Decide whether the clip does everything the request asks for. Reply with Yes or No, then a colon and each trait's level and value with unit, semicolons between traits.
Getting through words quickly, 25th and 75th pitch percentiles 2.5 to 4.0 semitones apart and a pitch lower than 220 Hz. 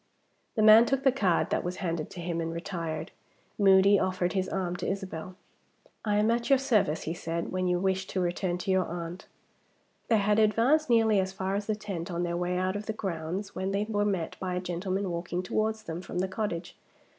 Yes: fast, 215 wpm; average, 3.0 semitones; high, 190 Hz